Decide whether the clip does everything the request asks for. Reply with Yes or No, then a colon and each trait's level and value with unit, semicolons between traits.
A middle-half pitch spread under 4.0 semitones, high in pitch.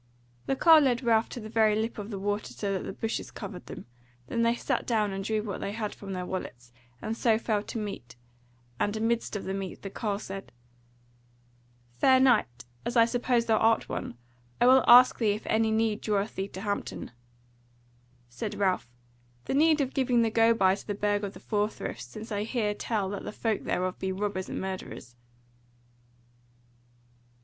Yes: average, 2.7 semitones; high, 215 Hz